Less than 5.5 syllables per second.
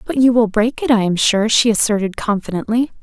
No: 5.6 syllables/s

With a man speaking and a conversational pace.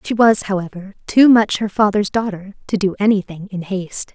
No: female; average, 190 wpm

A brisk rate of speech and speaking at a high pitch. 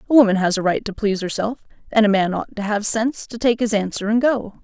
Yes: fast, 270 wpm; high, 215 Hz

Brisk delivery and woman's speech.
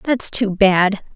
No: average, 155 wpm; female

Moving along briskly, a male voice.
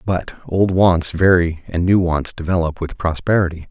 No: average, 160 wpm; male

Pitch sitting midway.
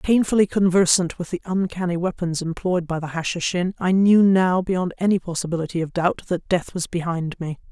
Yes: medium, 180 Hz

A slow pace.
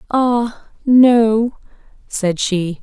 Yes: slow, 85 wpm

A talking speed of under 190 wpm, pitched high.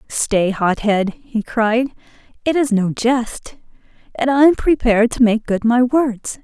Yes: average, 160 wpm; high, 235 Hz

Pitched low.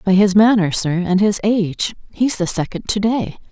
No: high, 195 Hz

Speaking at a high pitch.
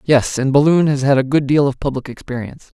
No: medium, 140 Hz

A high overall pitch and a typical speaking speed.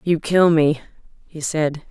No: medium, 155 Hz; average, 155 wpm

